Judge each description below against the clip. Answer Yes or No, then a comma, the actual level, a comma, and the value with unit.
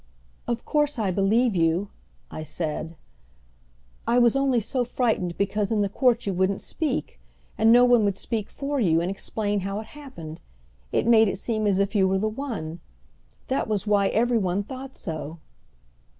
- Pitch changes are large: No, average, 4.2 semitones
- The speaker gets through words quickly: No, average, 180 wpm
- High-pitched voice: Yes, high, 210 Hz